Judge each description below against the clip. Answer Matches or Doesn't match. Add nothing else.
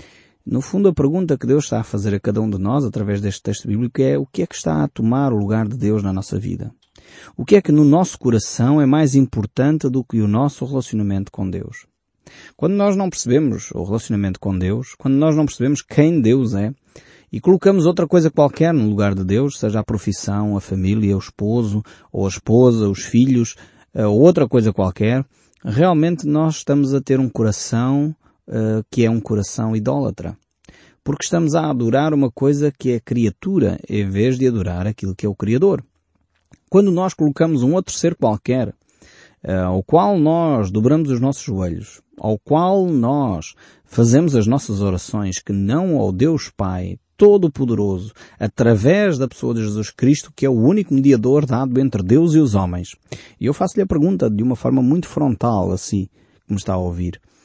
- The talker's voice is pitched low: Matches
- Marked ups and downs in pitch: Matches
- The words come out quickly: Matches